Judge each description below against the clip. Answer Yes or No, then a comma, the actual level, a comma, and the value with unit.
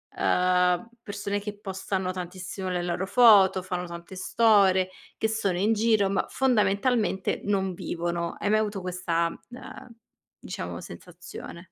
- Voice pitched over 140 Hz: Yes, high, 190 Hz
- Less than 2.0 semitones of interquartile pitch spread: No, narrow, 2.5 semitones